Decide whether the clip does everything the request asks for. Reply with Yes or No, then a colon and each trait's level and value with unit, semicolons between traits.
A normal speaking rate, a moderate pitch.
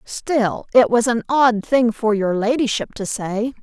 No: average, 180 wpm; high, 230 Hz